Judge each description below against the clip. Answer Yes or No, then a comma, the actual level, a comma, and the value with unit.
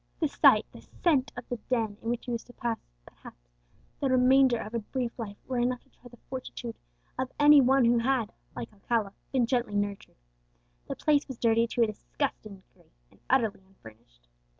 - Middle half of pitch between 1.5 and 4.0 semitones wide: Yes, average, 3.3 semitones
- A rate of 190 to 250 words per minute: Yes, average, 195 wpm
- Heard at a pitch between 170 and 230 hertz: No, high, 240 Hz